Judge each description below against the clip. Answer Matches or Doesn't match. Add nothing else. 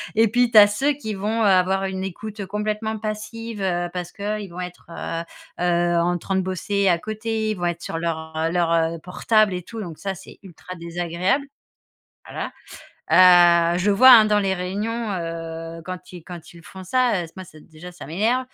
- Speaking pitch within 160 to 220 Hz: Matches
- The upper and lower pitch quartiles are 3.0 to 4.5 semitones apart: Matches